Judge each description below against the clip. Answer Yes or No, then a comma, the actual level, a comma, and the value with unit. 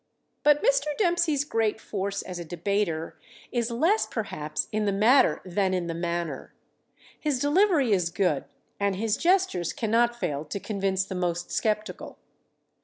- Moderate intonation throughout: No, wide, 6.4 semitones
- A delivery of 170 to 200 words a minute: No, average, 150 wpm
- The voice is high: Yes, high, 205 Hz